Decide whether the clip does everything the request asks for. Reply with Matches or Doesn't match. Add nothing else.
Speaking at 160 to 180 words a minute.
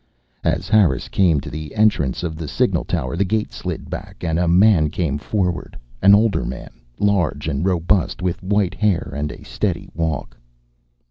Matches